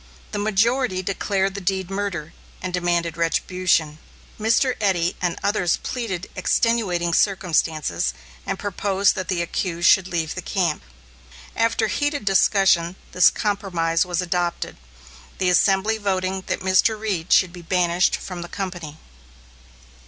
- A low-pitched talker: No, medium, 185 Hz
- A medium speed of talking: No, slow, 130 wpm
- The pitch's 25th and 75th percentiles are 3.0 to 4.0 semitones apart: No, narrow, 2.6 semitones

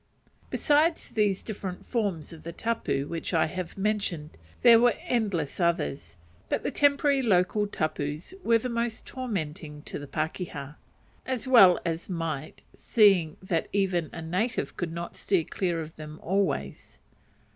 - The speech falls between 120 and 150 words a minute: Yes, average, 145 wpm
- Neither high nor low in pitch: Yes, medium, 180 Hz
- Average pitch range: No, wide, 5.7 semitones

